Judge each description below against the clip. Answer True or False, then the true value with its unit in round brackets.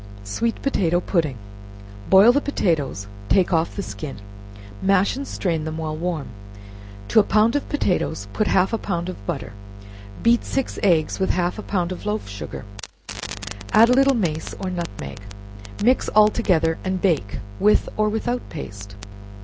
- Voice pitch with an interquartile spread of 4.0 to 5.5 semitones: True (5.0 semitones)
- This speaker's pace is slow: False (160 wpm)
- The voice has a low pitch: False (185 Hz)